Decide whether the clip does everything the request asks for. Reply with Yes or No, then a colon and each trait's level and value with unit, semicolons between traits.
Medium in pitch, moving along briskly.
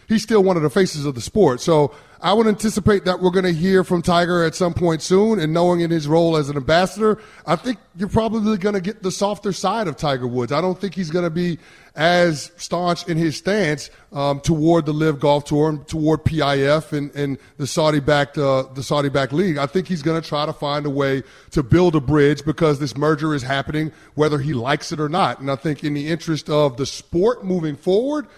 Yes: medium, 160 Hz; fast, 235 wpm